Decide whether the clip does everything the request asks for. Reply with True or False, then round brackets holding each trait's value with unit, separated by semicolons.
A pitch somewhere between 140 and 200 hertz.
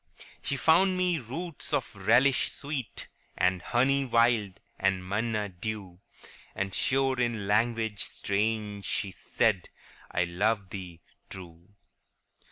False (110 Hz)